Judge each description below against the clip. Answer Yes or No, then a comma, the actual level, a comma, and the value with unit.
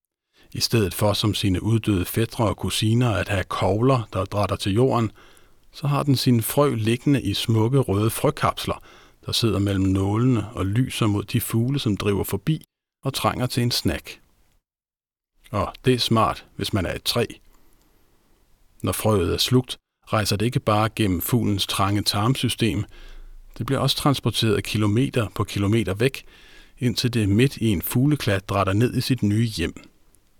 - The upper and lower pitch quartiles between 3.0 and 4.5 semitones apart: Yes, average, 3.7 semitones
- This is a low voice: Yes, low, 110 Hz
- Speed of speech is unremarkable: Yes, average, 165 wpm